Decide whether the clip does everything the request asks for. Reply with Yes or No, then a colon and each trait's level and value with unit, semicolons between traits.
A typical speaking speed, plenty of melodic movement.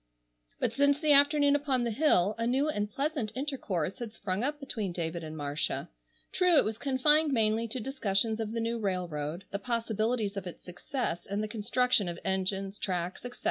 Yes: average, 185 wpm; wide, 5.8 semitones